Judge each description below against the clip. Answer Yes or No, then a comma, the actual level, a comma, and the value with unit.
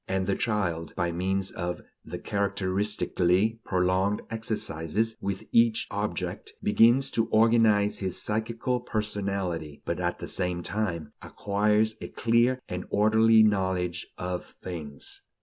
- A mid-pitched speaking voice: No, low, 100 Hz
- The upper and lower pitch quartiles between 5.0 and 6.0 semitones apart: No, average, 3.4 semitones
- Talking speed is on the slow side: Yes, slow, 125 wpm